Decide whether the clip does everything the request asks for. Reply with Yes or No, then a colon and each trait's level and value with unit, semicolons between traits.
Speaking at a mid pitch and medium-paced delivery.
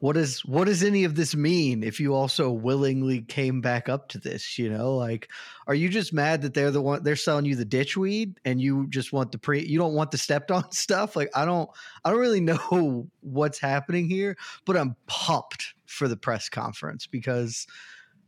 No: medium, 145 Hz; fast, 215 wpm